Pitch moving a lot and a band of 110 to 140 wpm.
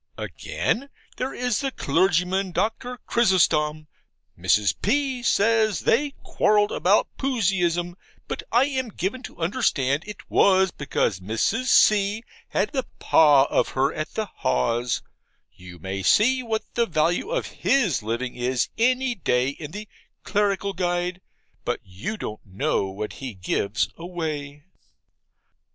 Yes: wide, 8.7 semitones; slow, 135 wpm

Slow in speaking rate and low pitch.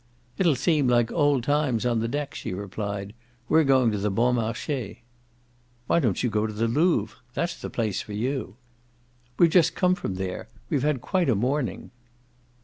No: average, 180 wpm; low, 125 Hz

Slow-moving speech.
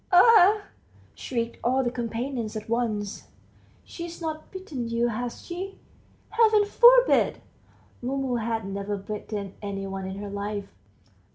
Yes: slow, 125 wpm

